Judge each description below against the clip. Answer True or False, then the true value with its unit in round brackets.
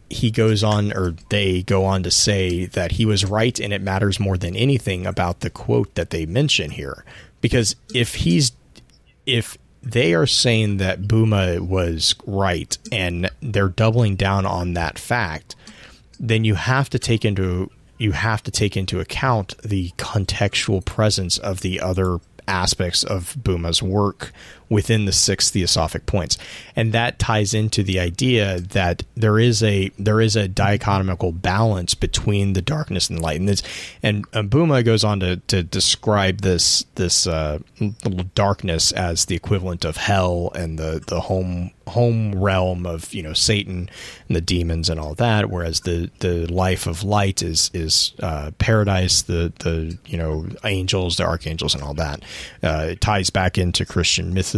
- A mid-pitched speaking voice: False (95 Hz)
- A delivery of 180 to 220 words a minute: False (170 wpm)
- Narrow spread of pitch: False (3.4 semitones)